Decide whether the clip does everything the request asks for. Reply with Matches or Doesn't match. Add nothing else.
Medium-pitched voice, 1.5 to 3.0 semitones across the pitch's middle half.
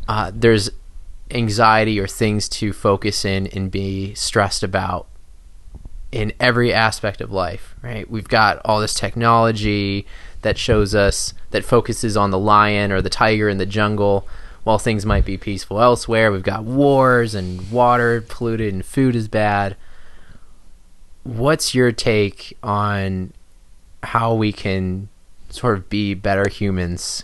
Doesn't match